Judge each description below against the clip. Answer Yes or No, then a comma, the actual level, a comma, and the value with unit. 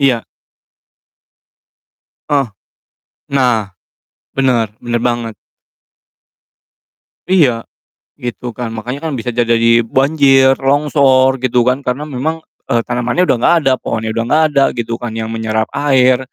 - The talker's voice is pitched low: Yes, low, 125 Hz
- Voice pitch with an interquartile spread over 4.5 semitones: No, average, 2.8 semitones